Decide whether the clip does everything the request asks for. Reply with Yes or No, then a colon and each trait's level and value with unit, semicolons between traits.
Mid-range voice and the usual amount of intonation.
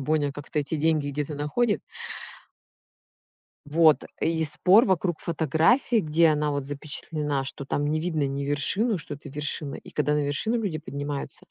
No: medium, 150 Hz; narrow, 2.2 semitones